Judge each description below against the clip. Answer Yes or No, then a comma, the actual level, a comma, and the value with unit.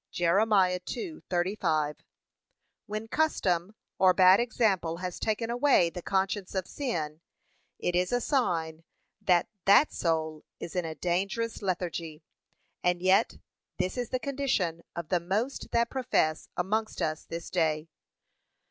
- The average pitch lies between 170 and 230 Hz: Yes, medium, 185 Hz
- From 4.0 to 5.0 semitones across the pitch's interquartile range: Yes, average, 4.7 semitones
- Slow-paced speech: Yes, slow, 130 wpm